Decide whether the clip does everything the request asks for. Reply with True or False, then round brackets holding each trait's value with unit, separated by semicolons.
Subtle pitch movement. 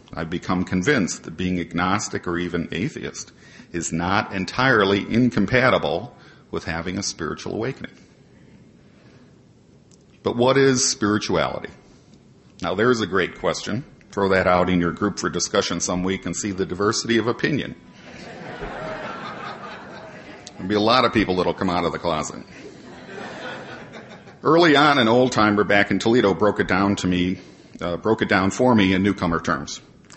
False (3.1 semitones)